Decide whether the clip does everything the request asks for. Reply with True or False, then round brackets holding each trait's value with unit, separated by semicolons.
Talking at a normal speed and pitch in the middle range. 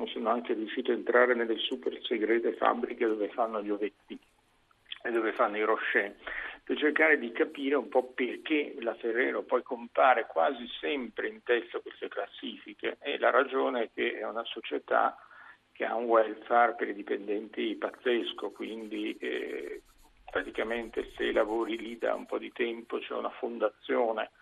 True (160 wpm; 160 Hz)